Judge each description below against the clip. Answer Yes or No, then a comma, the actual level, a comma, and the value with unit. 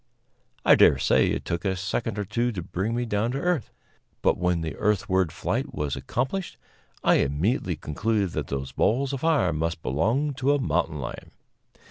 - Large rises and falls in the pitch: Yes, wide, 6.7 semitones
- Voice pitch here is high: No, low, 100 Hz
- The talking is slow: No, average, 180 wpm